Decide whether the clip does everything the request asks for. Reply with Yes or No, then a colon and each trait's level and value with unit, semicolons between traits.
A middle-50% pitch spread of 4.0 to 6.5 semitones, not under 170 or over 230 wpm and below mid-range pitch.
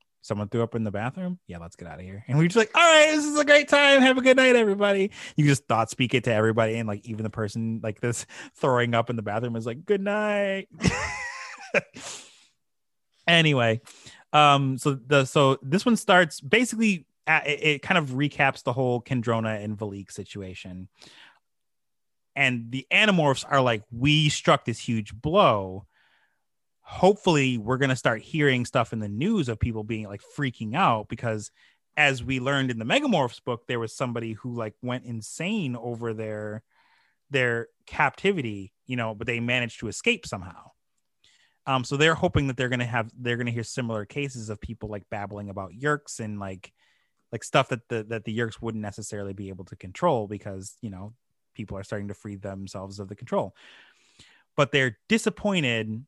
Yes: average, 5.2 semitones; average, 190 wpm; low, 120 Hz